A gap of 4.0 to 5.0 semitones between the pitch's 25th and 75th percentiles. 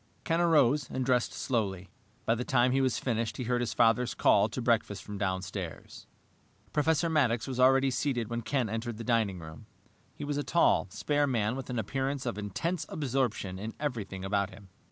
Yes: average, 4.3 semitones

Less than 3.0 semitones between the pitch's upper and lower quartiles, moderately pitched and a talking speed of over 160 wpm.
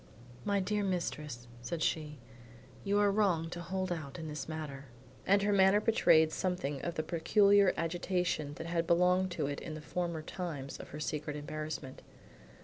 No: average, 3.6 semitones; medium, 170 Hz; average, 170 wpm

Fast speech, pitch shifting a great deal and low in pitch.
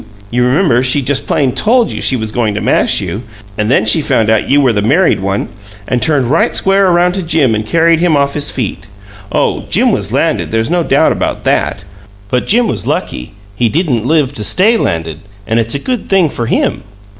Yes: fast, 215 wpm; wide, 7.0 semitones; low, 130 Hz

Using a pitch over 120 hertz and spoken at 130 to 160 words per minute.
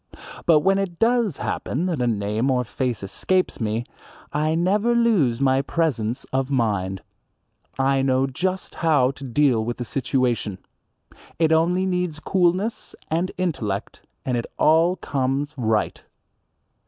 Yes: medium, 140 Hz; average, 140 wpm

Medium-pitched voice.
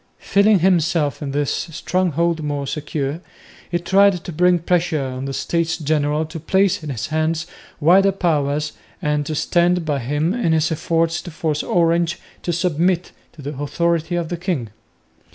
Yes: medium, 165 Hz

